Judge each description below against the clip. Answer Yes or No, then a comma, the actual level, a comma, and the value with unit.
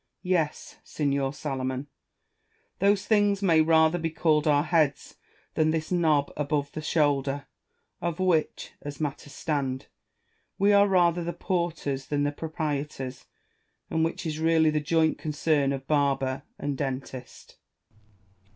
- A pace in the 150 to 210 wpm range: No, slow, 135 wpm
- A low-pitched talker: No, medium, 155 Hz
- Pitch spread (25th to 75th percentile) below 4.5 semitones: Yes, average, 2.7 semitones